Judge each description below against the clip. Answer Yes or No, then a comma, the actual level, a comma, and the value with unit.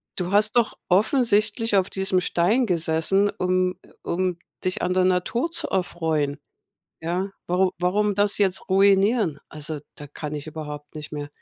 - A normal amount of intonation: Yes, average, 4.0 semitones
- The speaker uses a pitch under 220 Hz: Yes, medium, 185 Hz